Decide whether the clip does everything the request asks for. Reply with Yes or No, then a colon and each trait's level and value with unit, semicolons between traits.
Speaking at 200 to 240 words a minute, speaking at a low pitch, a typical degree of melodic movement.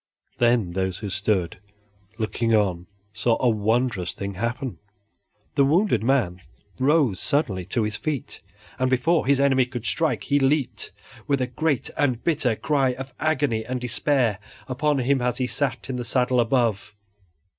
No: average, 155 wpm; low, 125 Hz; average, 4.0 semitones